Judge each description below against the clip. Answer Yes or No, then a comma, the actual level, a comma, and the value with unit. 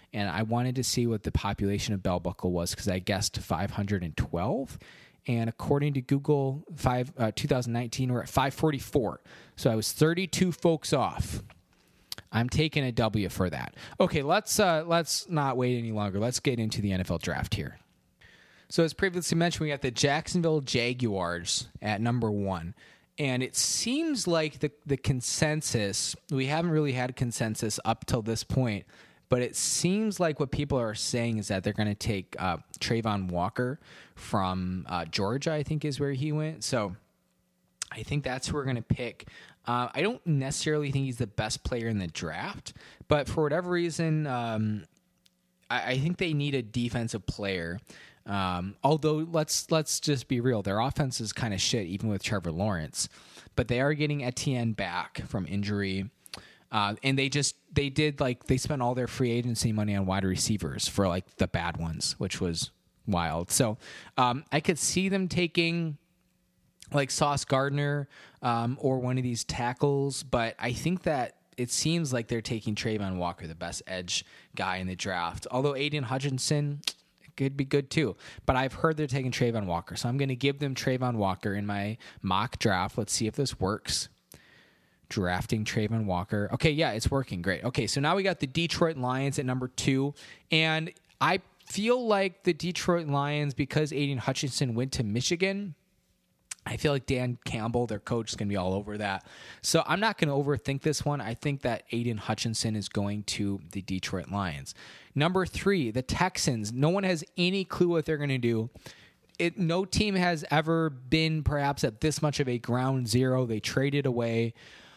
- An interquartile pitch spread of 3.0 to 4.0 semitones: No, wide, 5.6 semitones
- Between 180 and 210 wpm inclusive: Yes, average, 185 wpm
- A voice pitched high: No, low, 125 Hz